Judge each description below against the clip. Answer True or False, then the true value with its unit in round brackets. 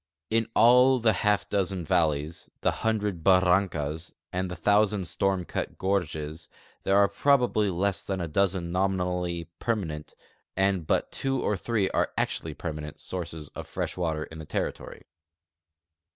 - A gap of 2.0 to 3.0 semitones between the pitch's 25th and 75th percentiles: False (3.4 semitones)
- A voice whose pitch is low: True (95 Hz)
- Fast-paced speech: False (145 wpm)